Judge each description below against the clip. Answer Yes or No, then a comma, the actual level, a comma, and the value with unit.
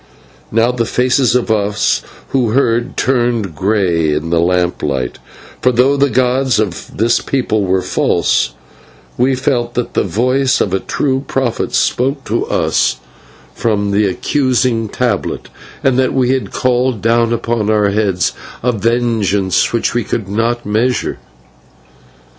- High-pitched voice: No, low, 115 Hz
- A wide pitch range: No, average, 3.8 semitones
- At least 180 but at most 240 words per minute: No, average, 140 wpm